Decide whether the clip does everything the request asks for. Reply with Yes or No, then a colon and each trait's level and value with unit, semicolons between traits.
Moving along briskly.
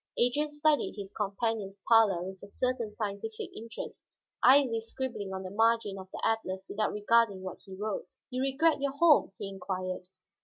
No: average, 165 wpm